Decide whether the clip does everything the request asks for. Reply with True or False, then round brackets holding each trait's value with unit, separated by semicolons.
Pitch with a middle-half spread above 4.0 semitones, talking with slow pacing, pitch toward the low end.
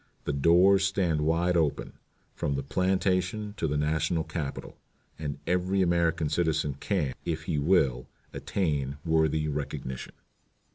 False (3.6 semitones; 130 wpm; 80 Hz)